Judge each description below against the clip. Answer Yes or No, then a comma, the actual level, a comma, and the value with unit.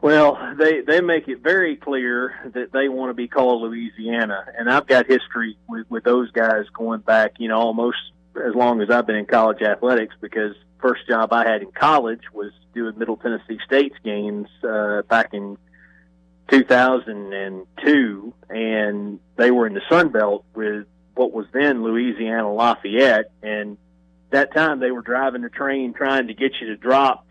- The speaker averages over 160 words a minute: Yes, average, 180 wpm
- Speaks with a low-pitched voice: Yes, low, 115 Hz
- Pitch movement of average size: Yes, average, 3.3 semitones